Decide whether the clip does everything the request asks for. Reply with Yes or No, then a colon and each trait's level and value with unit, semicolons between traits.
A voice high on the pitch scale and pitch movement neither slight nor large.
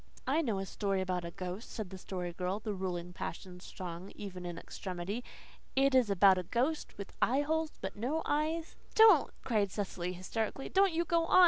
No: high, 200 Hz; wide, 7.2 semitones